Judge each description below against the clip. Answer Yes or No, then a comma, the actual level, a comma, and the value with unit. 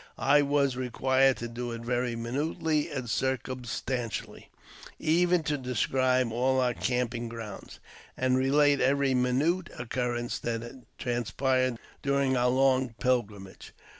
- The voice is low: Yes, low, 130 Hz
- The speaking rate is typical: No, slow, 130 wpm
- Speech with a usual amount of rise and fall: No, narrow, 2.1 semitones